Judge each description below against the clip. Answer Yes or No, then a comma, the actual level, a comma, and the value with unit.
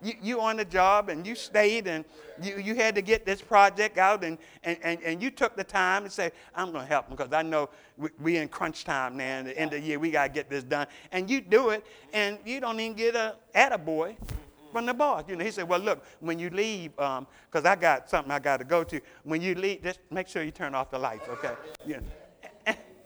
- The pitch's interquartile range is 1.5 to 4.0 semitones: No, wide, 5.5 semitones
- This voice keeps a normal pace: No, fast, 265 wpm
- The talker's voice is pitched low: No, medium, 180 Hz